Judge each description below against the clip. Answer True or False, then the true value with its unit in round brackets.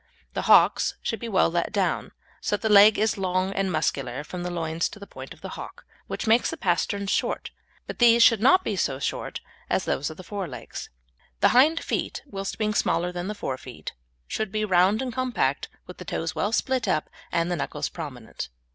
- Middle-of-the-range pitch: False (195 Hz)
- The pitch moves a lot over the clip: False (4.3 semitones)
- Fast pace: True (210 wpm)